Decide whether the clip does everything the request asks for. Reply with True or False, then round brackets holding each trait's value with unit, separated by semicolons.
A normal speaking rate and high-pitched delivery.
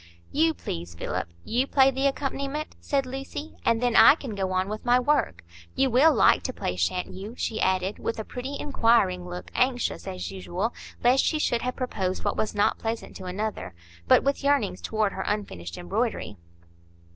True (180 wpm; 225 Hz)